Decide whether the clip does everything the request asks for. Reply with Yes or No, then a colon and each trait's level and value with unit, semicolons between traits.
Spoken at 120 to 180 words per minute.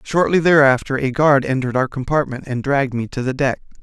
No: fast, 205 wpm